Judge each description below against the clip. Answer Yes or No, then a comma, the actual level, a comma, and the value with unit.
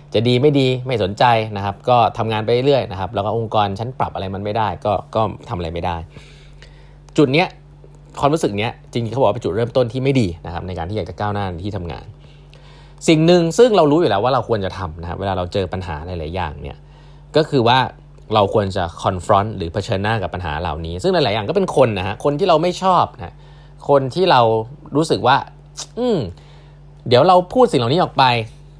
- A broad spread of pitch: Yes, wide, 6.9 semitones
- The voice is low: Yes, low, 115 Hz